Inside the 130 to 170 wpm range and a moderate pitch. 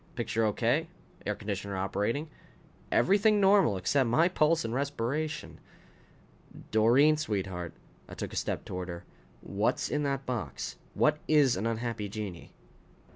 No: slow, 135 wpm; low, 115 Hz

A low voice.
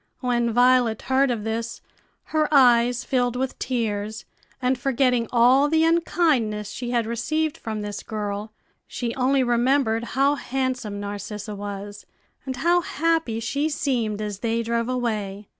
No: high, 240 Hz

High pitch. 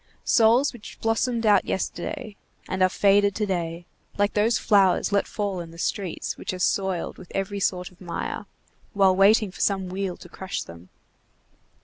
Yes: high, 195 Hz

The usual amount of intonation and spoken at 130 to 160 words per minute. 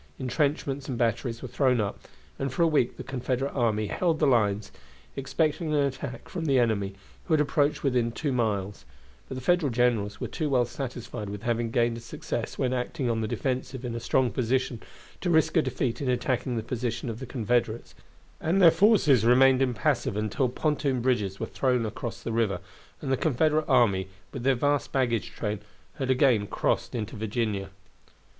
No: average, 3.1 semitones; average, 185 wpm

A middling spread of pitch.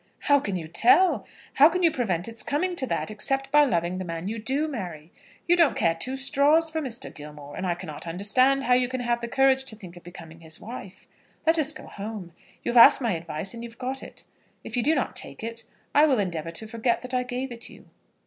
No: wide, 7.1 semitones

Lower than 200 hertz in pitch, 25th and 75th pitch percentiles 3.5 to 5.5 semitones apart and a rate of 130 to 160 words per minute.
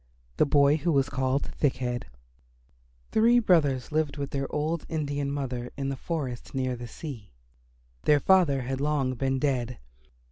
No: medium, 140 Hz; narrow, 2.6 semitones; average, 155 wpm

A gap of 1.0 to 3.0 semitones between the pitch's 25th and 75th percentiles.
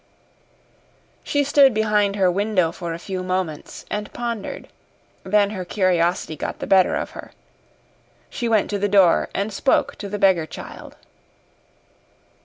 Yes: narrow, 2.6 semitones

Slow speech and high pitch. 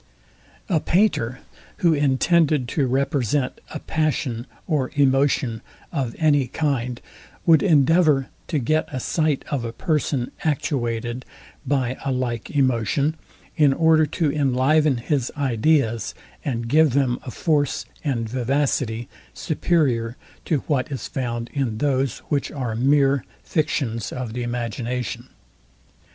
No: slow, 125 wpm; low, 135 Hz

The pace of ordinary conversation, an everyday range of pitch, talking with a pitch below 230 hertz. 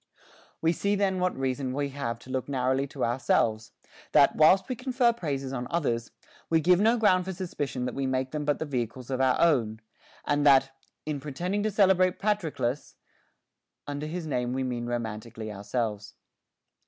No: average, 180 wpm; wide, 6.2 semitones; medium, 140 Hz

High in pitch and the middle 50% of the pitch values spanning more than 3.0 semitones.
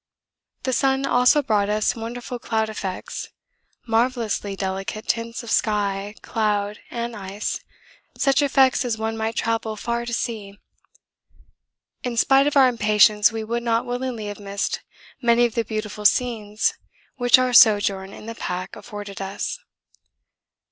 No: high, 225 Hz; average, 2.7 semitones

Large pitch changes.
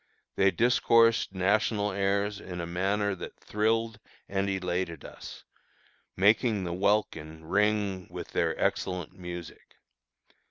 No: average, 2.7 semitones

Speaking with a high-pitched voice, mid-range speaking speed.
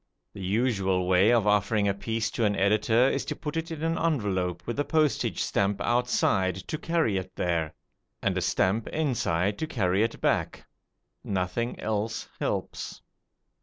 No: low, 105 Hz; average, 165 wpm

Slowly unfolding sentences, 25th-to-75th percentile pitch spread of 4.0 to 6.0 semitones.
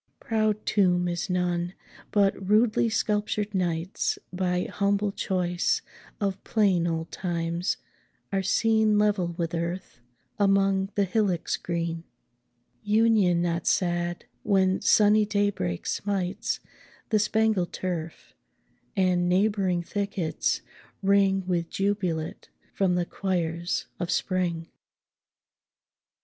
No: slow, 105 wpm; average, 2.8 semitones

